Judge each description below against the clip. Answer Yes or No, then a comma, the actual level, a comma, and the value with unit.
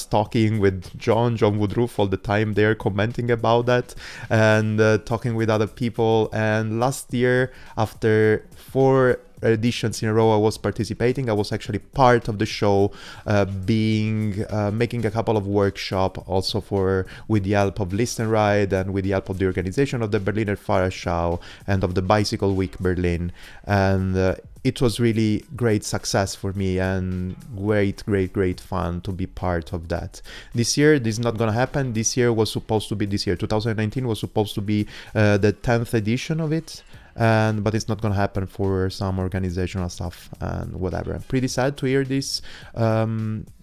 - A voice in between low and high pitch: No, low, 110 Hz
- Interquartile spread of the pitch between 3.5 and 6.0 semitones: No, average, 2.9 semitones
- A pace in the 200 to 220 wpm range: No, average, 185 wpm